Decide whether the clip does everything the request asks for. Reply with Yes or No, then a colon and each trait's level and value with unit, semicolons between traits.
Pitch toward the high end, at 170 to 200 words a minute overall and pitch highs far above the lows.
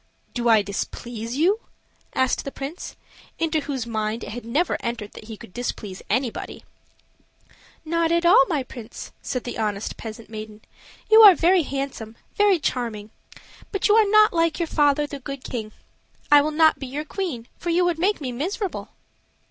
Yes: very high, 275 Hz; average, 175 wpm; wide, 6.6 semitones